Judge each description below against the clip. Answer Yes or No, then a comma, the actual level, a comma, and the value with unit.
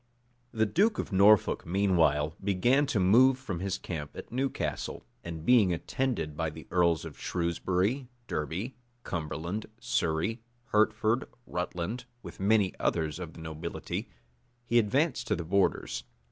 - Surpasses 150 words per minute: No, average, 140 wpm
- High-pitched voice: No, very low, 95 Hz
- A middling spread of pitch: No, wide, 5.9 semitones